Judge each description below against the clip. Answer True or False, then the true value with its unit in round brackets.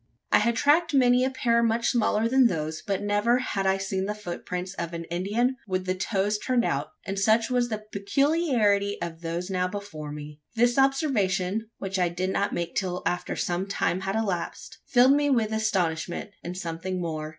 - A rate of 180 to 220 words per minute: True (190 wpm)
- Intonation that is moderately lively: True (4.6 semitones)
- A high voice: True (200 Hz)